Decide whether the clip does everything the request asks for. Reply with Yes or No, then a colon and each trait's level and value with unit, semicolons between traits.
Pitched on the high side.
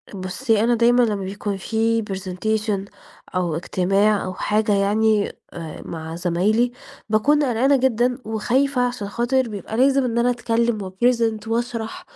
Yes: high, 220 Hz